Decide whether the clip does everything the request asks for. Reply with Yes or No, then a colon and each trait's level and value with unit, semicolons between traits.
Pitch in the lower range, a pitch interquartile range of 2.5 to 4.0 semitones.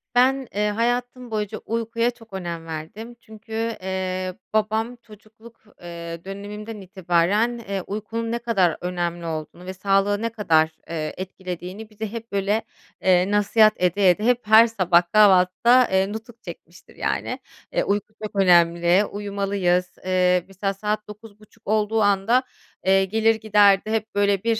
No: high, 205 Hz; average, 3.1 semitones